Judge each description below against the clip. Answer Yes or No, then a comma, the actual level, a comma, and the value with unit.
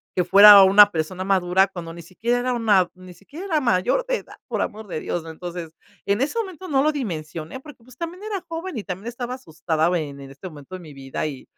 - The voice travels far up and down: Yes, wide, 7.2 semitones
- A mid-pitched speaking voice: No, high, 195 Hz